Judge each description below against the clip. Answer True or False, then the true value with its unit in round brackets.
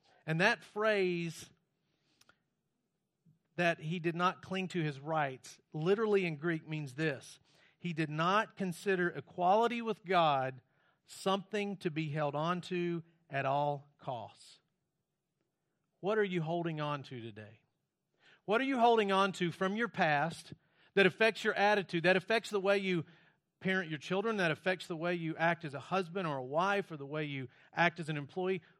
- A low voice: False (170 Hz)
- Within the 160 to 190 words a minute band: True (165 wpm)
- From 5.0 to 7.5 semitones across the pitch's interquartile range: False (3.6 semitones)